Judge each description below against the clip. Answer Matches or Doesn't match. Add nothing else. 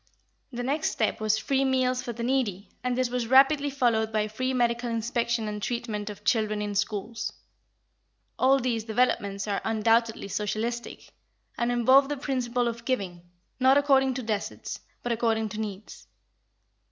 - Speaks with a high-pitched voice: Matches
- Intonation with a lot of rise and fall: Doesn't match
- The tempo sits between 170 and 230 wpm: Doesn't match